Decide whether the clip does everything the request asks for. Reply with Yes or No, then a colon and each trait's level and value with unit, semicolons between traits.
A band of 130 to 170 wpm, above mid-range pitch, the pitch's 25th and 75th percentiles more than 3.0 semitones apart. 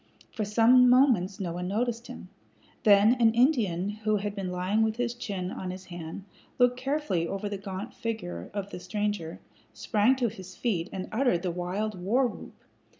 No: average, 180 wpm; high, 205 Hz; average, 4.2 semitones